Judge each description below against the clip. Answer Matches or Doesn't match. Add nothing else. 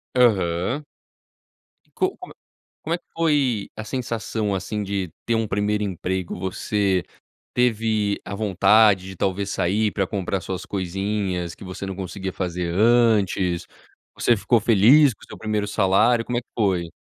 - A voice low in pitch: Matches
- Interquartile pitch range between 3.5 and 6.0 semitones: Doesn't match